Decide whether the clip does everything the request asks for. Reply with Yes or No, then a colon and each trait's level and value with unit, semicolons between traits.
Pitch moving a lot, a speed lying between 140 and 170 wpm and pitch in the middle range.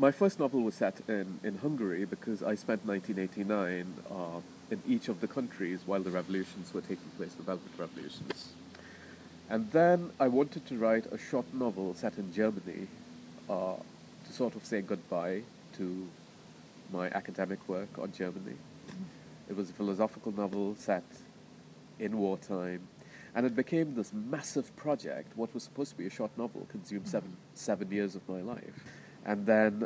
No: wide, 5.9 semitones; average, 165 wpm; low, 105 Hz